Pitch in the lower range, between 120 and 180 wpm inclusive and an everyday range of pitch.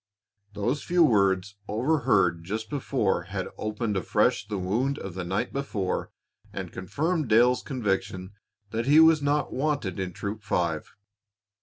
No: low, 110 Hz; average, 140 wpm; wide, 6.2 semitones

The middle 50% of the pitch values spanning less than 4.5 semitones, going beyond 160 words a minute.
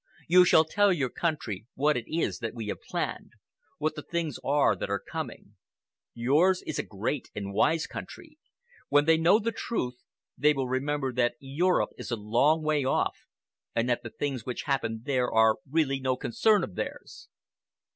No: average, 5.0 semitones; average, 180 wpm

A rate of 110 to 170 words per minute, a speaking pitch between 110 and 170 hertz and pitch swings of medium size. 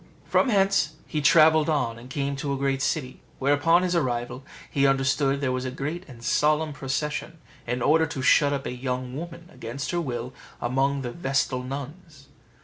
No: average, 185 wpm; medium, 140 Hz; average, 3.2 semitones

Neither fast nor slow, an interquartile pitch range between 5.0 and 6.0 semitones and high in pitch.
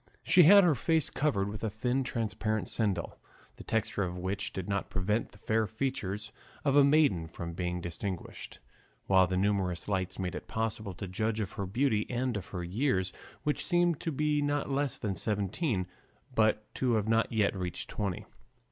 No: average, 180 wpm; wide, 5.6 semitones; low, 105 Hz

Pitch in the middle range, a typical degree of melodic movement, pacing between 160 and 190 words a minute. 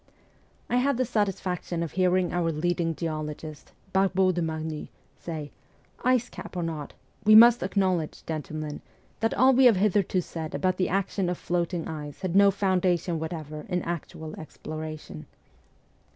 No: medium, 175 Hz; average, 3.4 semitones; average, 150 wpm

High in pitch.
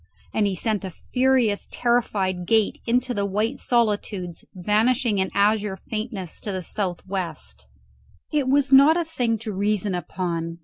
Yes: high, 210 Hz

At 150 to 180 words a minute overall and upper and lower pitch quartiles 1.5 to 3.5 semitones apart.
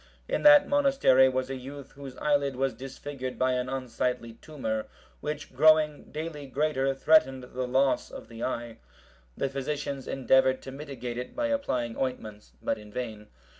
Yes: average, 160 wpm; narrow, 2.5 semitones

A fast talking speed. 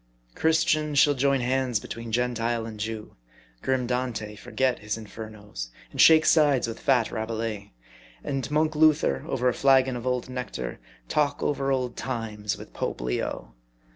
No: average, 150 wpm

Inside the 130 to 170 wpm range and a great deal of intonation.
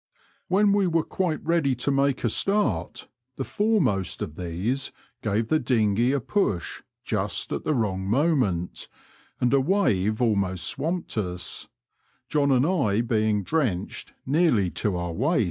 Yes: average, 145 wpm; wide, 7.9 semitones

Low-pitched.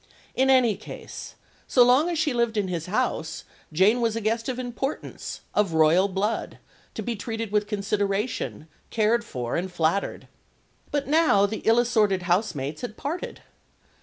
No: high, 215 Hz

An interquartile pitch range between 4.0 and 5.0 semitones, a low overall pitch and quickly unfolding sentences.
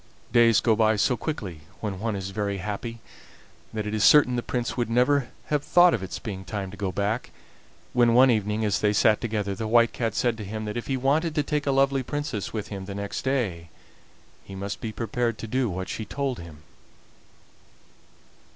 No: average, 3.6 semitones; low, 110 Hz; fast, 210 wpm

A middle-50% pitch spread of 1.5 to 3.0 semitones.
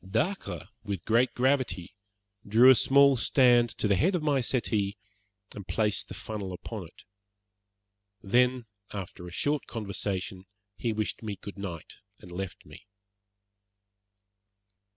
No: average, 4.5 semitones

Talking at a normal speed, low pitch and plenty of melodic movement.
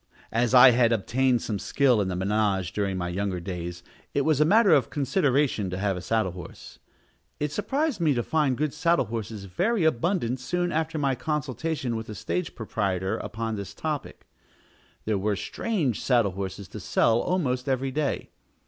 Yes: average, 175 wpm; low, 120 Hz; wide, 6.9 semitones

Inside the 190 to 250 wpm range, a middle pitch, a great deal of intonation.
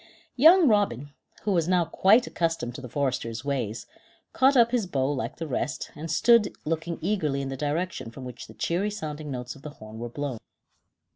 Yes: average, 195 wpm; medium, 150 Hz; wide, 6.4 semitones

